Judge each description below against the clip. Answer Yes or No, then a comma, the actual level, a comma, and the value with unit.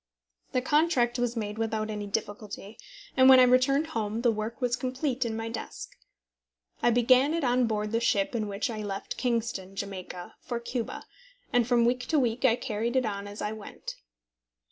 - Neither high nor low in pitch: No, high, 235 Hz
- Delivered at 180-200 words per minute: Yes, average, 190 wpm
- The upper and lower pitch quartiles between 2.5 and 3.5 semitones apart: Yes, average, 3.0 semitones